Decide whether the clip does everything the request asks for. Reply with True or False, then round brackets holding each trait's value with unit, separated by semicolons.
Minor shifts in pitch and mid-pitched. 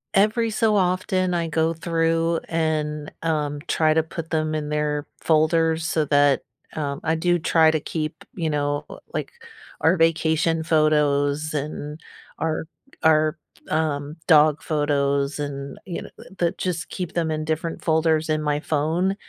True (1.7 semitones; 160 Hz)